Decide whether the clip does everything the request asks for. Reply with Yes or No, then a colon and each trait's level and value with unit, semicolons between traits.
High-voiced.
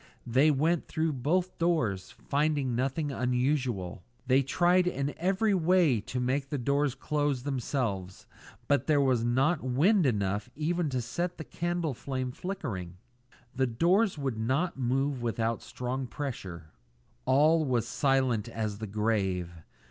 No: low, 135 Hz